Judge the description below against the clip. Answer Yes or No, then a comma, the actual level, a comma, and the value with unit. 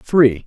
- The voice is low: Yes, low, 130 Hz